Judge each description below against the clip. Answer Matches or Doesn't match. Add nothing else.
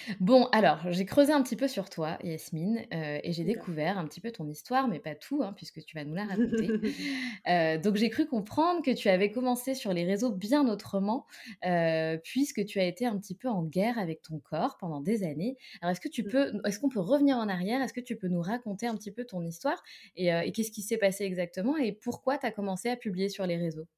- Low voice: Doesn't match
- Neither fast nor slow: Doesn't match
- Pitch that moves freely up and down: Matches